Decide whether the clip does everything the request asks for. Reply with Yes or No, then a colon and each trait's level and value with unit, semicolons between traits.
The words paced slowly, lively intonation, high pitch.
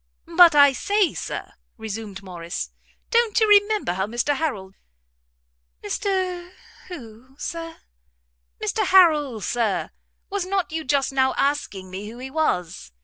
Yes: slow, 130 wpm; wide, 8.8 semitones; very high, 280 Hz